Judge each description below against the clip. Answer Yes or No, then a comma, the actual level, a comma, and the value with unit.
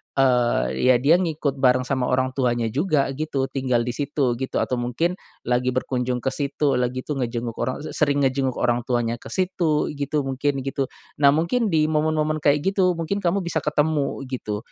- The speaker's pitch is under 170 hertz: Yes, low, 135 Hz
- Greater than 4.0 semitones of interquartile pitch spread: No, average, 3.5 semitones